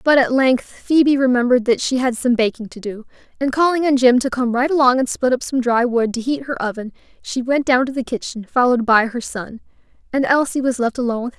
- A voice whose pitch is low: No, very high, 250 Hz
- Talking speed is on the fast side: Yes, fast, 255 wpm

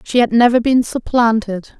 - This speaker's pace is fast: No, average, 170 wpm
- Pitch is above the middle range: Yes, high, 230 Hz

